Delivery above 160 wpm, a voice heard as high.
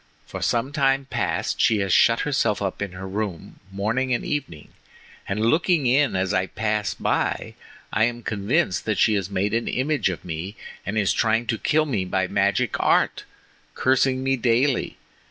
No: average, 175 wpm; low, 110 Hz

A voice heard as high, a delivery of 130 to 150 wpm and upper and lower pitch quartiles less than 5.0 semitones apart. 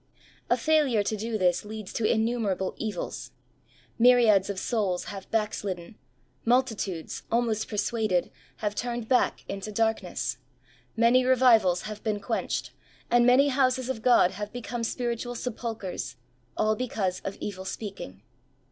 Yes: high, 220 Hz; slow, 135 wpm; average, 3.6 semitones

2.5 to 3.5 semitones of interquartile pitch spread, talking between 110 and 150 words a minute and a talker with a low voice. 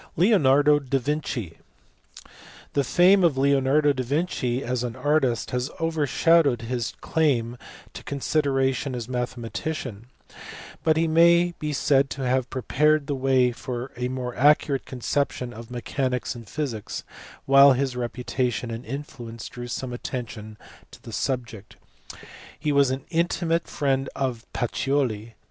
Yes: average, 3.2 semitones; average, 140 wpm; low, 130 Hz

